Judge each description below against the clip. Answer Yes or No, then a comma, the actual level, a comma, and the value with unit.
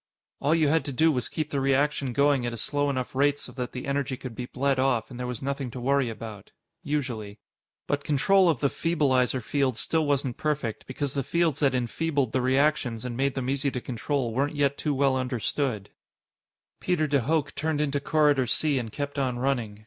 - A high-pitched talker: No, low, 135 Hz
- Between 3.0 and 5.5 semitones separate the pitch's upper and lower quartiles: No, narrow, 2.6 semitones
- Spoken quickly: Yes, fast, 210 wpm